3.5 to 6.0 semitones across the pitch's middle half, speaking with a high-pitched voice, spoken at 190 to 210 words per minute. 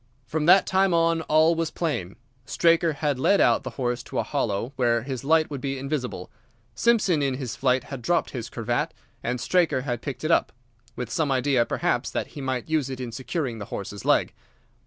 No: average, 4.6 semitones; low, 135 Hz; average, 200 wpm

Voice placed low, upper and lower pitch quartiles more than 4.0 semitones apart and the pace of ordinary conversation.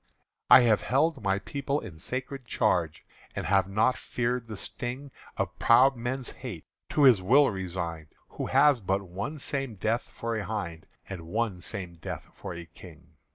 Yes: low, 110 Hz; wide, 5.6 semitones; average, 170 wpm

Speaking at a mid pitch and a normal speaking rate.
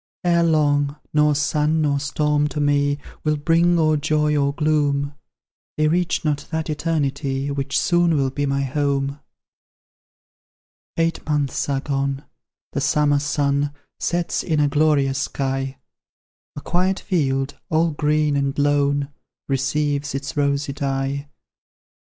No: medium, 145 Hz; slow, 130 wpm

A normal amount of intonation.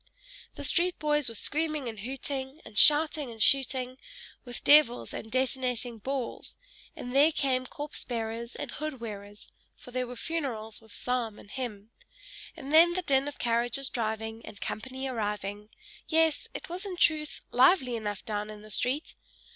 Yes: average, 4.7 semitones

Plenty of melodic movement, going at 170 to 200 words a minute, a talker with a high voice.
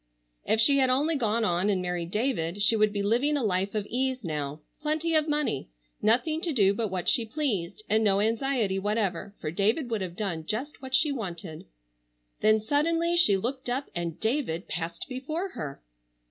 Yes: wide, 6.4 semitones; average, 180 wpm; high, 220 Hz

